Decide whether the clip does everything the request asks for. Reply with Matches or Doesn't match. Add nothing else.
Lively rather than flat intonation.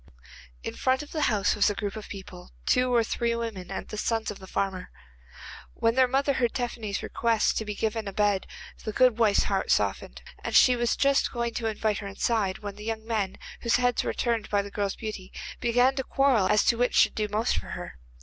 Doesn't match